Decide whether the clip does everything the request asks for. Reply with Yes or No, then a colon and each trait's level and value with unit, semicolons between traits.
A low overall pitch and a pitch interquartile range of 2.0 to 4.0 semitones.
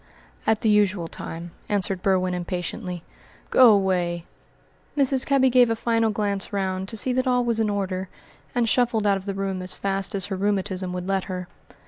No: high, 195 Hz; average, 3.3 semitones